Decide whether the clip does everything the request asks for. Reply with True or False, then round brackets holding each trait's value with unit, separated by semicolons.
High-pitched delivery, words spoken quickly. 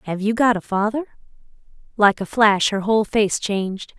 False (210 Hz; 180 wpm)